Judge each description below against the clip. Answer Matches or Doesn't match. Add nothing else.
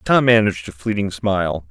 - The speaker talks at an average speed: Matches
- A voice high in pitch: Doesn't match